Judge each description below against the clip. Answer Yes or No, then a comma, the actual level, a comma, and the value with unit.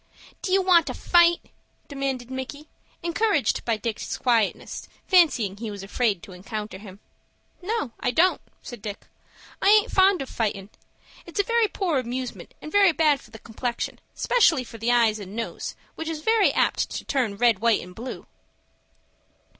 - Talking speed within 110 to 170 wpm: Yes, average, 165 wpm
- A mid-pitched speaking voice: No, very high, 250 Hz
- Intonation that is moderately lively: No, wide, 7.7 semitones